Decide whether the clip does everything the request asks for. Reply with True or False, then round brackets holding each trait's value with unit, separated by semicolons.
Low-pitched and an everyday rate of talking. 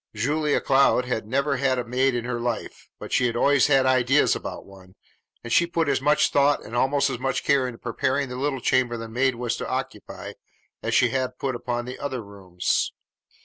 False (130 Hz; 210 wpm)